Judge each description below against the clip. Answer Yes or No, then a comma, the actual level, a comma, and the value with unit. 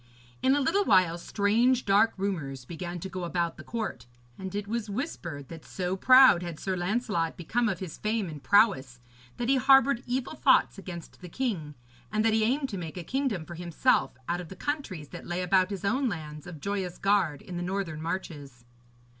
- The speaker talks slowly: No, average, 200 wpm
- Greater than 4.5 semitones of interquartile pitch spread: Yes, average, 5.0 semitones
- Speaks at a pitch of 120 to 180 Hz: No, high, 190 Hz